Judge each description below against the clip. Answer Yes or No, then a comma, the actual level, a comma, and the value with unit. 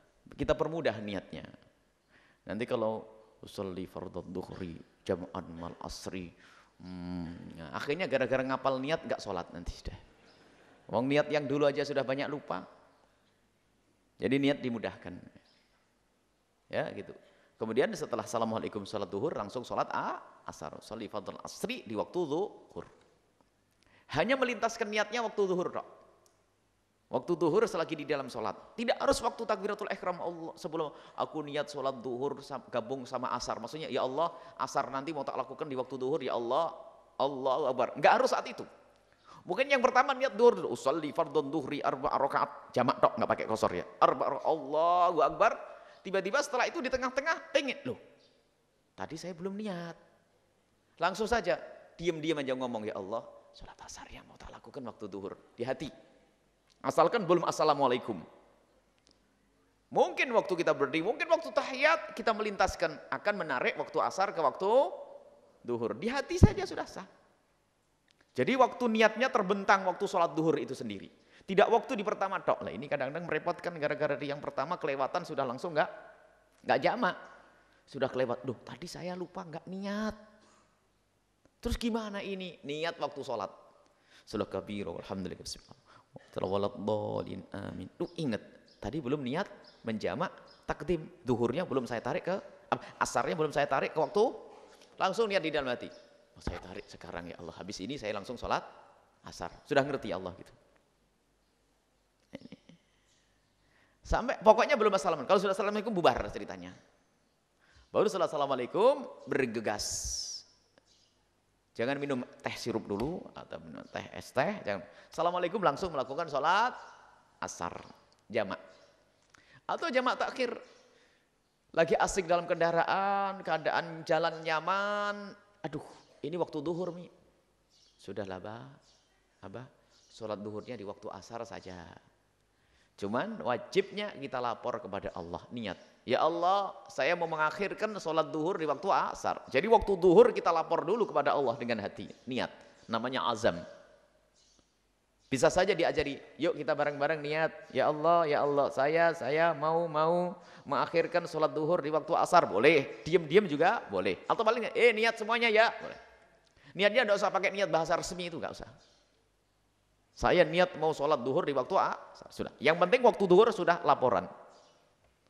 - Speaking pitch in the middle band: Yes, medium, 165 Hz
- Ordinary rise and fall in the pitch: No, wide, 7.9 semitones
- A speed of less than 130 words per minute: No, fast, 140 wpm